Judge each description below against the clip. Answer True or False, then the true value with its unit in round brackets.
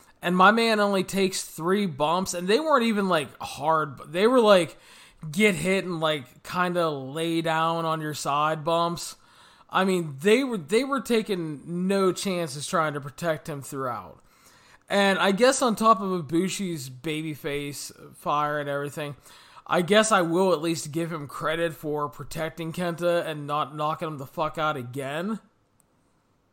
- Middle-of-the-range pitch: True (165 Hz)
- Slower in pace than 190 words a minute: True (170 wpm)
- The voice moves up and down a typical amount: True (3.9 semitones)